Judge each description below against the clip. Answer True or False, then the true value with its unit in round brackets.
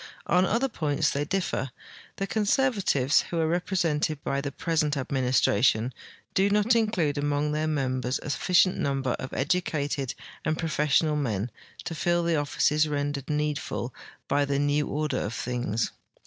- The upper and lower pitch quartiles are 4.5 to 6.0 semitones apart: False (3.7 semitones)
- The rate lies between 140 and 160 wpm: True (150 wpm)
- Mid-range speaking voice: True (150 Hz)